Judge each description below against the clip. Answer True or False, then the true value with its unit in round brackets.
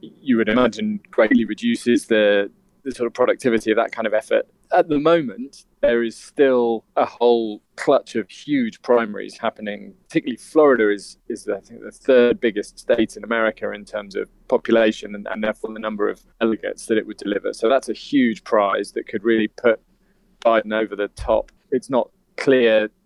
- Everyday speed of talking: True (185 wpm)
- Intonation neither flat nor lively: False (5.7 semitones)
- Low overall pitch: True (115 Hz)